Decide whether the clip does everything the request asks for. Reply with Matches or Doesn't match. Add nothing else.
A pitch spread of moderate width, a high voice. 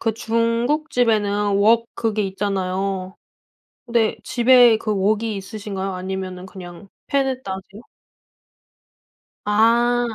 Matches